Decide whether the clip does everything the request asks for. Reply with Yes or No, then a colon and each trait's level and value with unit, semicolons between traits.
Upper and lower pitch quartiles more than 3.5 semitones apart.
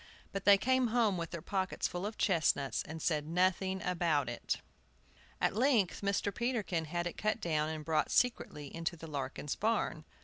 Yes: average, 4.5 semitones